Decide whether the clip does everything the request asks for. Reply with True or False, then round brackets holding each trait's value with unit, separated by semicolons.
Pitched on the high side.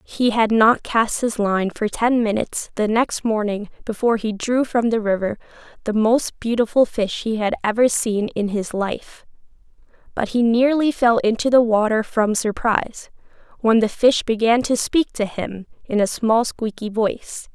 True (225 Hz)